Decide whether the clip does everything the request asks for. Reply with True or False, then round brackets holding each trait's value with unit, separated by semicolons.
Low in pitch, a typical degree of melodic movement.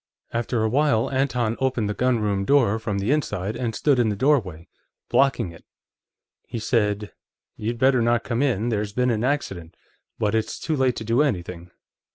True (115 Hz; 3.8 semitones)